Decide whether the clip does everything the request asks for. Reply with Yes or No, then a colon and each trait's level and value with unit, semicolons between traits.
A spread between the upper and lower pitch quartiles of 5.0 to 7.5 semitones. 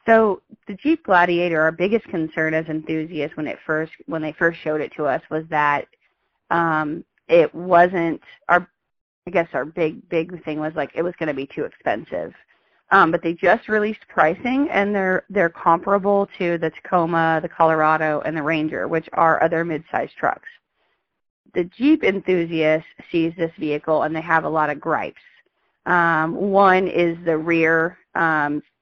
No: average, 2.8 semitones